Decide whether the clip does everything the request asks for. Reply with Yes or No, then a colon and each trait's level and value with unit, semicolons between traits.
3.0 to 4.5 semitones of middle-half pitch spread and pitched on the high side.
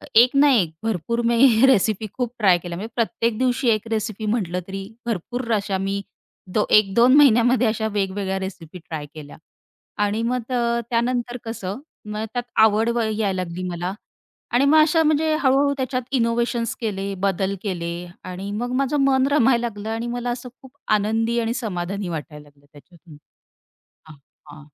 Yes: average, 4.1 semitones; high, 220 Hz